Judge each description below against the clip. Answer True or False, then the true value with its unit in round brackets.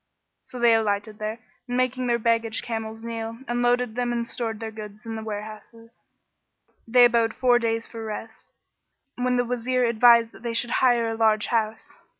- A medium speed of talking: True (175 wpm)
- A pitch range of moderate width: False (1.5 semitones)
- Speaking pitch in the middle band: False (230 Hz)